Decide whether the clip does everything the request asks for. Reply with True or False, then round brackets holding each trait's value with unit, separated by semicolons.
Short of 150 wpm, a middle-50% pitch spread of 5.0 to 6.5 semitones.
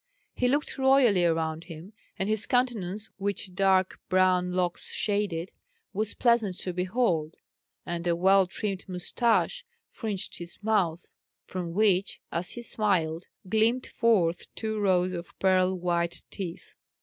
False (135 wpm; 3.6 semitones)